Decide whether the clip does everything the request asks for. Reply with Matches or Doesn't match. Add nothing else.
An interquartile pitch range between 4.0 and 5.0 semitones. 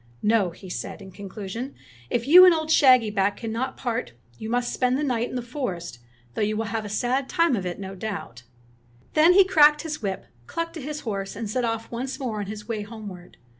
Matches